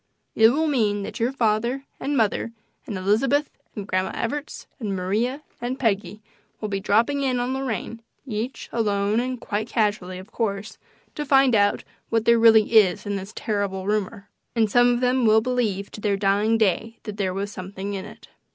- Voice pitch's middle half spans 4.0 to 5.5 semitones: No, average, 3.3 semitones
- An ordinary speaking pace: Yes, average, 185 wpm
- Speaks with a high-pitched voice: Yes, high, 220 Hz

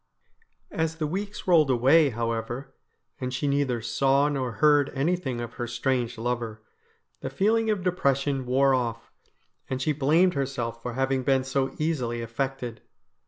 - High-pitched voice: No, low, 135 Hz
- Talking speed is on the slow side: No, average, 155 wpm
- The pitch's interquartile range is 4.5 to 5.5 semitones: No, average, 3.5 semitones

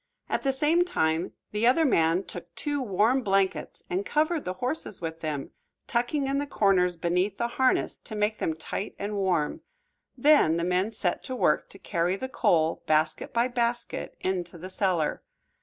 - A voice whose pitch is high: Yes, high, 195 Hz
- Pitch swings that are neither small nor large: No, wide, 6.7 semitones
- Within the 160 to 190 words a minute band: Yes, average, 175 wpm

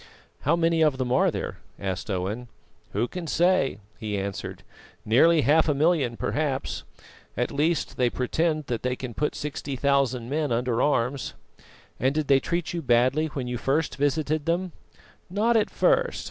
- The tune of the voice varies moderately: Yes, average, 4.4 semitones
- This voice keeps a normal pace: Yes, average, 165 wpm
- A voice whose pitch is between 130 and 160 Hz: Yes, medium, 140 Hz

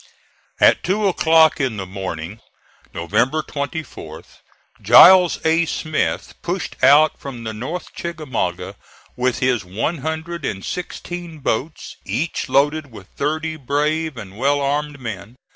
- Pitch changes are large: Yes, wide, 5.8 semitones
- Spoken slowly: Yes, slow, 125 wpm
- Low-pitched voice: No, medium, 145 Hz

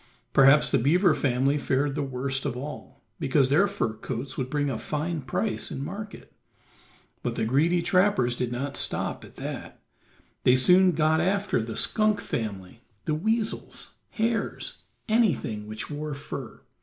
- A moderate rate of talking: Yes, average, 155 wpm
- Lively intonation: Yes, wide, 5.7 semitones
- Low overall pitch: No, medium, 145 Hz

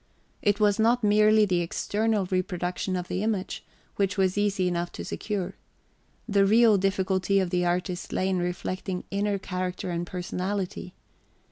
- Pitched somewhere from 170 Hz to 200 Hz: Yes, high, 190 Hz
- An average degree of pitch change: No, narrow, 2.2 semitones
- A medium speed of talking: Yes, average, 150 wpm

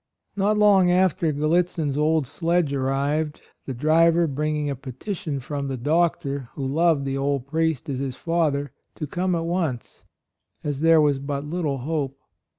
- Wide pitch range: No, average, 3.2 semitones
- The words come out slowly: No, average, 165 wpm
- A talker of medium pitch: Yes, medium, 150 Hz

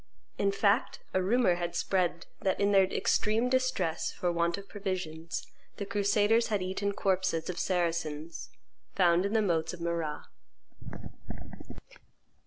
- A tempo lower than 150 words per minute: Yes, slow, 135 wpm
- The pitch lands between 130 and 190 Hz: Yes, medium, 185 Hz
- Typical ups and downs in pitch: Yes, average, 3.0 semitones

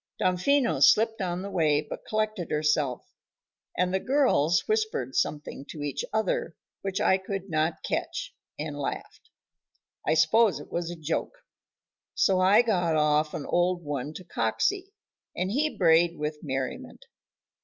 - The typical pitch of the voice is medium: Yes, medium, 175 Hz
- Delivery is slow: No, average, 145 wpm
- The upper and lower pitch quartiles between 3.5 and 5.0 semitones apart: No, wide, 5.6 semitones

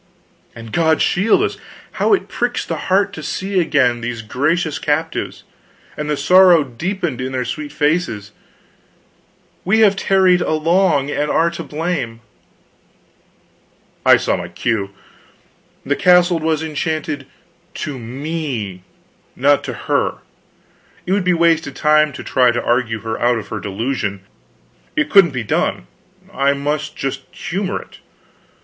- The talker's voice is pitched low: No, medium, 150 Hz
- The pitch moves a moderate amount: No, wide, 5.9 semitones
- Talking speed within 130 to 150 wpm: Yes, average, 140 wpm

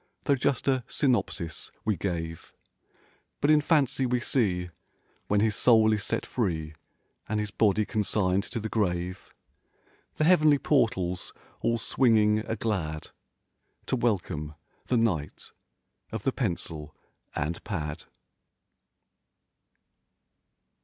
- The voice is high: No, low, 105 Hz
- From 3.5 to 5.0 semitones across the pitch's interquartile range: No, wide, 5.6 semitones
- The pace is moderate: No, slow, 115 wpm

